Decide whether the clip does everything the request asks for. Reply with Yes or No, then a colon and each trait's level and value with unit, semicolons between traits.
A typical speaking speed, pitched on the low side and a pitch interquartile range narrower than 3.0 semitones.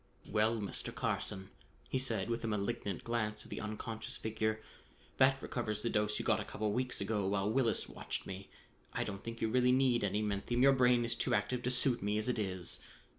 No: fast, 215 wpm; low, 110 Hz; narrow, 2.5 semitones